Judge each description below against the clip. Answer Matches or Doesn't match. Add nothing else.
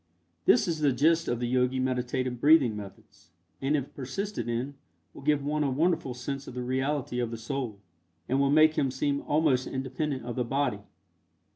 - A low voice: Matches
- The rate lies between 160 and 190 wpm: Matches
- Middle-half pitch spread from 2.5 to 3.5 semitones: Matches